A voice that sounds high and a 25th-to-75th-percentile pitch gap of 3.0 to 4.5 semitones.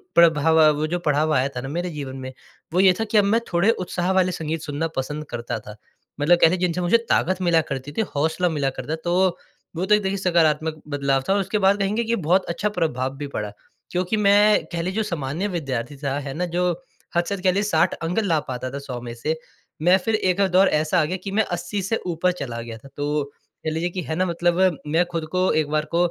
No: medium, 170 Hz; average, 4.1 semitones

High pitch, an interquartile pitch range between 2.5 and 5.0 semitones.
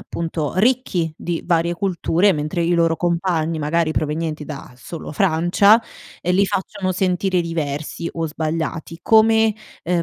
No: medium, 170 Hz; average, 2.8 semitones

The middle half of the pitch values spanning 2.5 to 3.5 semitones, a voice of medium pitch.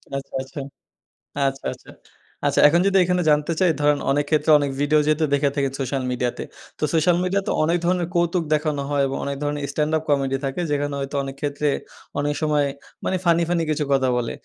Yes: average, 2.9 semitones; medium, 150 Hz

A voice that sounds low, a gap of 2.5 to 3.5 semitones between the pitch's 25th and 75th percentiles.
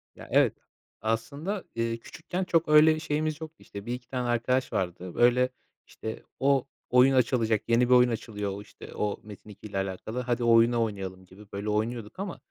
No: low, 120 Hz; average, 3.9 semitones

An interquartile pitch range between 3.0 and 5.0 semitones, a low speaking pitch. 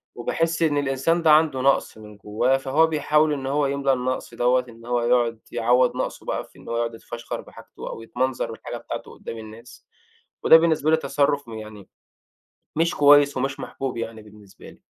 Yes: average, 3.9 semitones; low, 130 Hz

